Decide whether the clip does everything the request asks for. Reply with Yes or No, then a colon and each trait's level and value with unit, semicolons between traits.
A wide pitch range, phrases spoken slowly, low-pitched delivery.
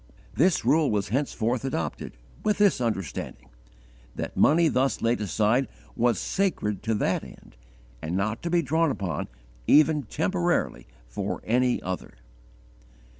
Yes: wide, 7.2 semitones; slow, 130 wpm; low, 125 Hz